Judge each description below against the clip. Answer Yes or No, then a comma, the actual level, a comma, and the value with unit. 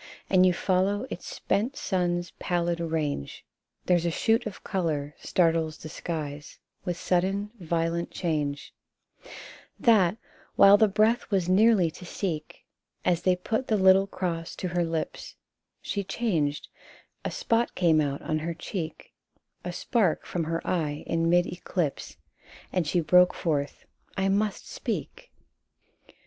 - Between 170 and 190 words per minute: No, average, 145 wpm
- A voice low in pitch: No, medium, 175 Hz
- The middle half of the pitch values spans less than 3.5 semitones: Yes, average, 3.0 semitones